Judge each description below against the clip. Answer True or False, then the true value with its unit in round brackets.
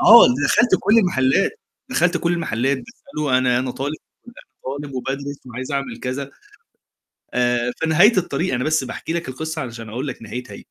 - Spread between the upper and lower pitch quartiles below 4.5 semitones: False (5.2 semitones)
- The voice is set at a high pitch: False (140 Hz)